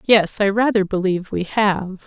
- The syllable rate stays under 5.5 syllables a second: Yes, 4.6 syllables/s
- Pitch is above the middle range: Yes, high, 200 Hz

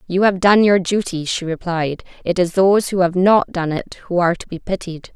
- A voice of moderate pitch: Yes, medium, 180 Hz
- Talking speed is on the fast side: Yes, fast, 235 wpm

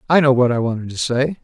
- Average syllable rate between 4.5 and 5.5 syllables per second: No, 6.6 syllables/s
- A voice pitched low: Yes, low, 130 Hz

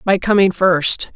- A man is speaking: No, female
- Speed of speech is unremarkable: Yes, average, 155 wpm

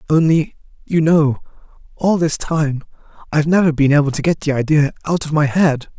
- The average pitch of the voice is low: No, medium, 150 Hz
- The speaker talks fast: No, average, 180 wpm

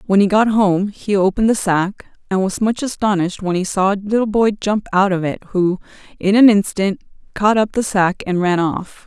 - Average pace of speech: No, fast, 220 wpm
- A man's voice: No, female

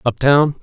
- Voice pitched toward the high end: No, medium, 140 Hz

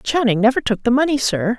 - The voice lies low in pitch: No, high, 240 Hz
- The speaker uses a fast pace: Yes, fast, 225 wpm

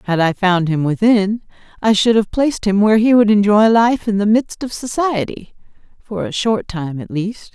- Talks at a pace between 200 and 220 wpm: Yes, fast, 205 wpm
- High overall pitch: Yes, high, 210 Hz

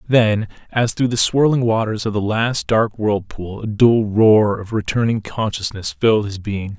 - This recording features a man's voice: Yes, male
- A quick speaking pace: No, average, 175 wpm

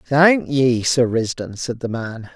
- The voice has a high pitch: No, low, 130 Hz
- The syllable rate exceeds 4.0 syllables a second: No, 3.7 syllables/s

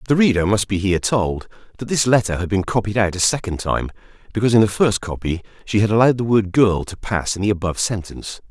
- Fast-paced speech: Yes, fast, 235 wpm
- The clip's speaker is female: No, male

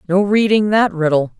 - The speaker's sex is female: Yes, female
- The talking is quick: No, average, 170 wpm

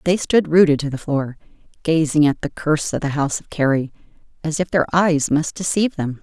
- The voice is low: No, medium, 155 Hz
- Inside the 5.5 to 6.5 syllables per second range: Yes, 5.7 syllables/s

